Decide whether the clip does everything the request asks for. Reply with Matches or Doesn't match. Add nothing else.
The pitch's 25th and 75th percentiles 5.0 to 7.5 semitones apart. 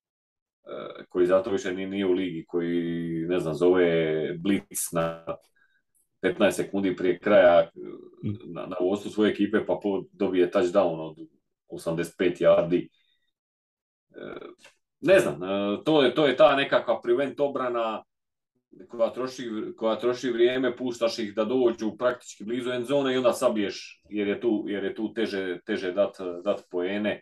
Matches